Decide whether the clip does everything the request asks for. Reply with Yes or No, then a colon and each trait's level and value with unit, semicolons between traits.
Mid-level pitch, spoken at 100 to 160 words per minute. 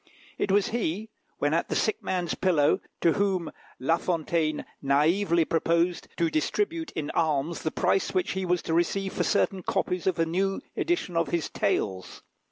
No: medium, 170 Hz; average, 175 wpm